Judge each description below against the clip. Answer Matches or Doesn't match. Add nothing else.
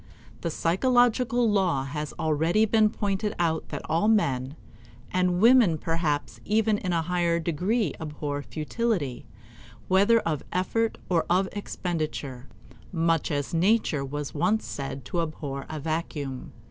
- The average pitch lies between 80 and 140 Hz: Doesn't match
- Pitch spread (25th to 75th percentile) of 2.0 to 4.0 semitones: Doesn't match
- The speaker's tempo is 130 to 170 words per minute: Matches